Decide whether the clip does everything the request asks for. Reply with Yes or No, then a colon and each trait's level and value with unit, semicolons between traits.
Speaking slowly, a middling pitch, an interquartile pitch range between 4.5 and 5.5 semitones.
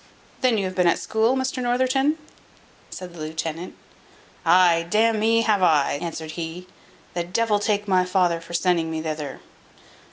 No: average, 165 wpm; medium, 180 Hz; average, 4.9 semitones